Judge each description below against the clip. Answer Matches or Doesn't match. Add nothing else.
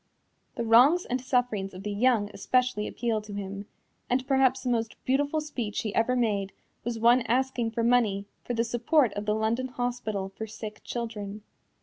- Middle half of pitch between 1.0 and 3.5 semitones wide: Matches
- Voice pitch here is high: Matches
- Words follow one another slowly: Doesn't match